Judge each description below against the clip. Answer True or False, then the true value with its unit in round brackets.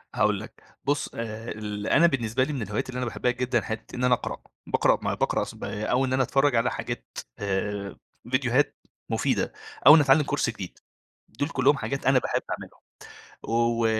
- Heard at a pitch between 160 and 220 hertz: False (125 Hz)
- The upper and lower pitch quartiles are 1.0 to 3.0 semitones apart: False (3.4 semitones)